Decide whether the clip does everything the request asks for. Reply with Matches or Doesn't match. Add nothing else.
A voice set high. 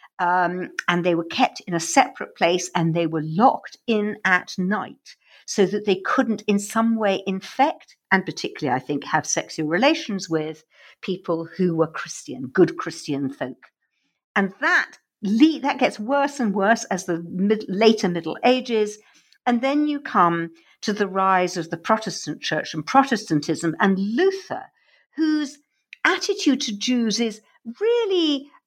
Matches